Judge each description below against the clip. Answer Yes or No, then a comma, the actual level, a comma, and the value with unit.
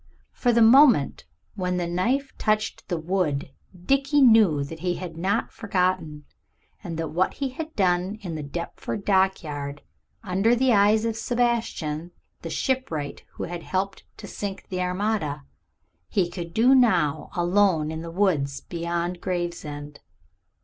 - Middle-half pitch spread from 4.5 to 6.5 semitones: Yes, average, 4.9 semitones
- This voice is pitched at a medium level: Yes, medium, 180 Hz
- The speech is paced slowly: No, average, 150 wpm